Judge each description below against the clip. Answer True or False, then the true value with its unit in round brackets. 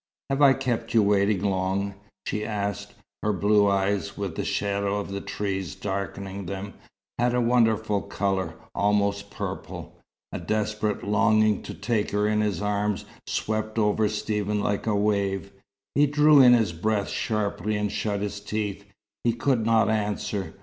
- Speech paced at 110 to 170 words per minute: True (155 wpm)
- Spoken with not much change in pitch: True (1.4 semitones)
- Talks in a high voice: False (105 Hz)